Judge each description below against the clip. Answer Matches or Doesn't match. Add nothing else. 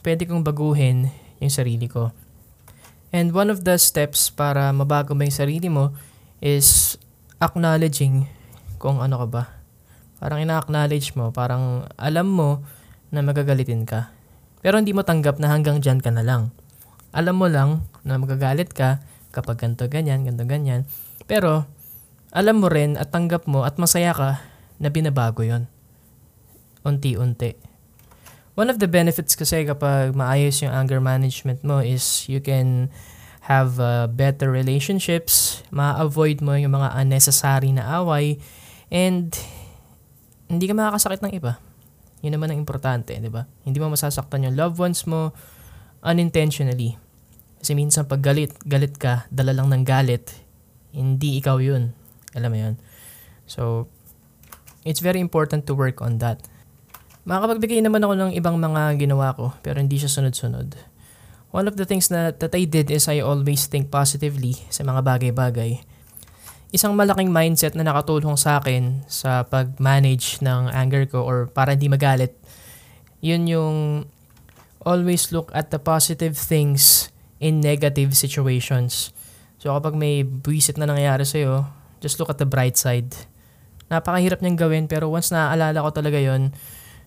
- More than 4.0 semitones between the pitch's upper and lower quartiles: Doesn't match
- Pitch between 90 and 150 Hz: Matches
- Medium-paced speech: Matches